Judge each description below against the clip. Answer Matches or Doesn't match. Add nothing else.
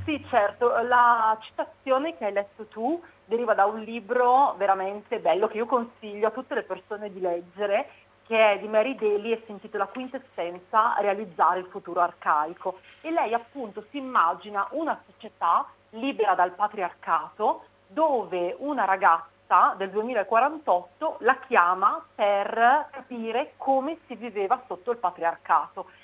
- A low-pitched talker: Doesn't match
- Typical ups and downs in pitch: Matches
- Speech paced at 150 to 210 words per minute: Doesn't match